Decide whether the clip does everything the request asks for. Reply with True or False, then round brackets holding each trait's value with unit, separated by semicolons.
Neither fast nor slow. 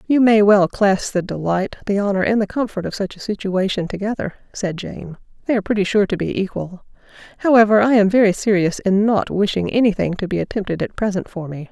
False (215 wpm)